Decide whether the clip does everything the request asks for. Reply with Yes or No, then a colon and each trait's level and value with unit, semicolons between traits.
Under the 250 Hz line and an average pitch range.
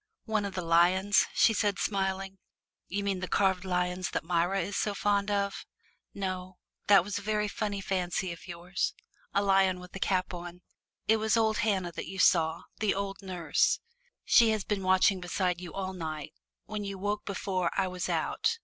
No: high, 190 Hz; narrow, 2.0 semitones